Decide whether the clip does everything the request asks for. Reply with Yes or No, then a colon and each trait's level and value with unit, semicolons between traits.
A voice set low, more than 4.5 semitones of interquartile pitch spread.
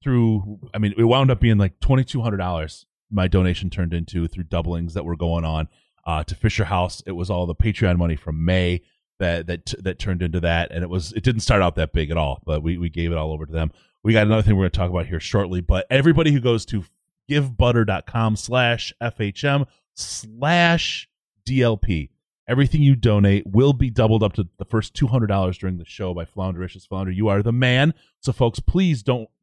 Yes: low, 100 Hz; wide, 5.4 semitones